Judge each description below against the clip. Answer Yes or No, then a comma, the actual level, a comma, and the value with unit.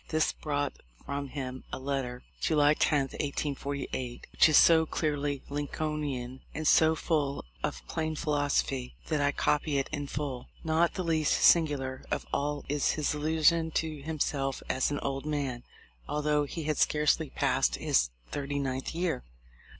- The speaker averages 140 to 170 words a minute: Yes, average, 150 wpm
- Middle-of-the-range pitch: Yes, medium, 145 Hz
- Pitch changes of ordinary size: No, narrow, 2.1 semitones